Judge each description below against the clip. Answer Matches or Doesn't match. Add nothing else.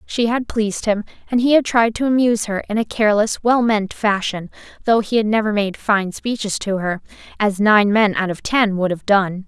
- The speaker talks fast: Matches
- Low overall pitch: Doesn't match